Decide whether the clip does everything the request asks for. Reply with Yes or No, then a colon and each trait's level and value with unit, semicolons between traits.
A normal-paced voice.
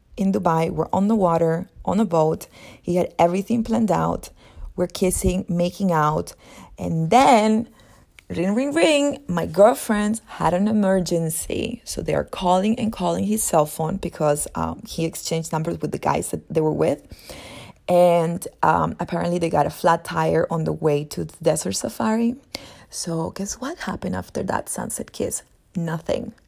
Yes: average, 165 wpm